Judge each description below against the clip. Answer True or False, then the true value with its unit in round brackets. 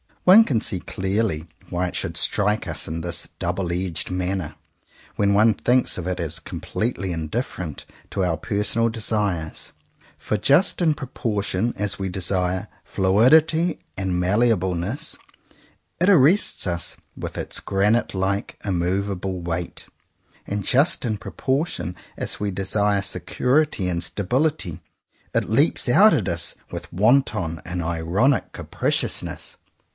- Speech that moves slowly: True (130 wpm)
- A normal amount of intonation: True (4.9 semitones)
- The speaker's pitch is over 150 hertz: False (100 Hz)